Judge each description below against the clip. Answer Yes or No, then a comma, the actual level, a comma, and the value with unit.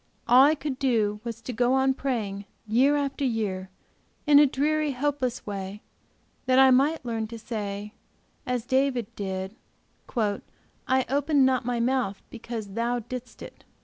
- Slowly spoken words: No, average, 150 wpm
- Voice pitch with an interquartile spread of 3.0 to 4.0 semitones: Yes, average, 3.7 semitones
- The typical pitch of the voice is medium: No, high, 245 Hz